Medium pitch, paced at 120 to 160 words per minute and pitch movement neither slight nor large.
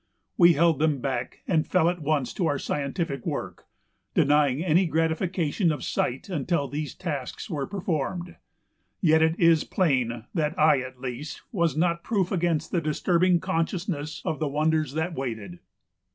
Yes: medium, 160 Hz; average, 155 wpm; average, 3.3 semitones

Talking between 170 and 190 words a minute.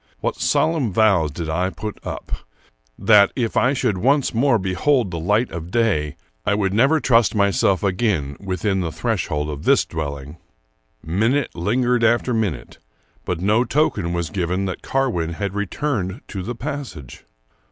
No: average, 155 wpm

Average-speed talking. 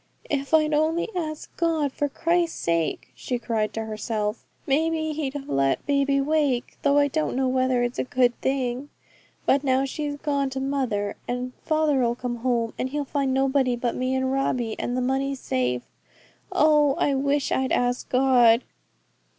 Yes: average, 170 wpm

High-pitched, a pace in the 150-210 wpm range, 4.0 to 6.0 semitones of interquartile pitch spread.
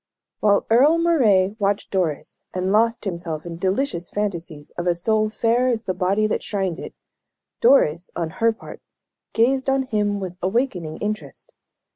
Yes: high, 205 Hz; average, 155 wpm; average, 4.5 semitones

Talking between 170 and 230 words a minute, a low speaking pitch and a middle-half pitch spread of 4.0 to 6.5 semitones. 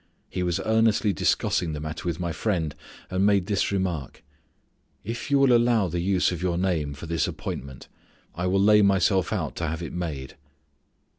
No: average, 180 wpm; very low, 90 Hz; average, 3.6 semitones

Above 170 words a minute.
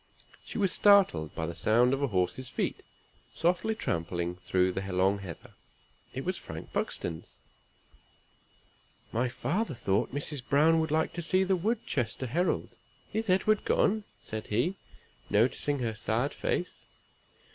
No: average, 140 wpm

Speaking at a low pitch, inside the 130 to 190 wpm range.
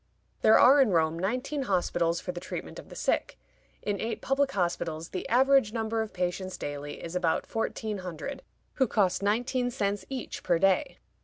No: high, 200 Hz; average, 175 wpm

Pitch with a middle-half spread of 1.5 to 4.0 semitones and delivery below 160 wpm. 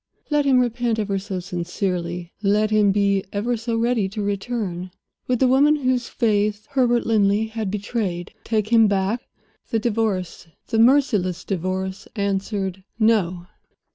Yes: average, 3.4 semitones; average, 140 wpm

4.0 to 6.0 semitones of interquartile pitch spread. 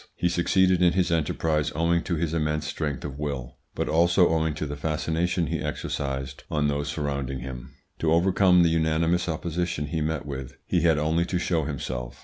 No: average, 2.8 semitones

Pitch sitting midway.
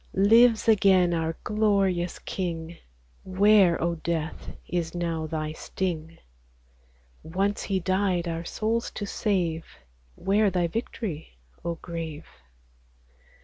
Yes: medium, 175 Hz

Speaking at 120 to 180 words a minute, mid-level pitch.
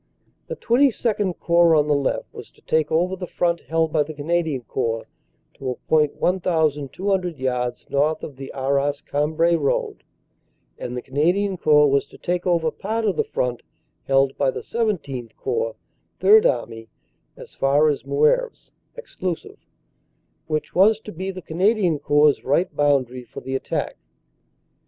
Yes: average, 155 wpm; medium, 155 Hz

